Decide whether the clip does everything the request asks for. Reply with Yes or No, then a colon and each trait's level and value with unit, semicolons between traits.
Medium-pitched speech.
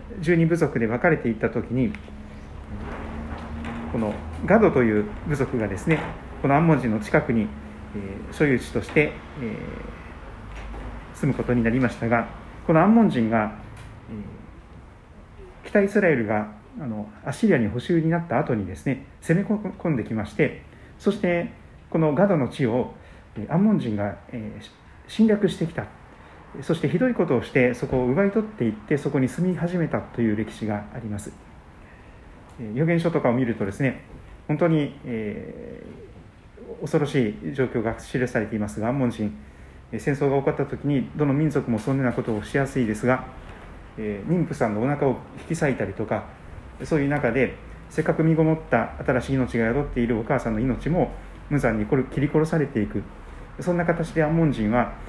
No: low, 120 Hz